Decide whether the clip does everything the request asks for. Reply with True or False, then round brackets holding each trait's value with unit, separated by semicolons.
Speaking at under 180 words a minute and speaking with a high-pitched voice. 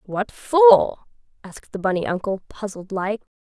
True (140 wpm; 210 Hz)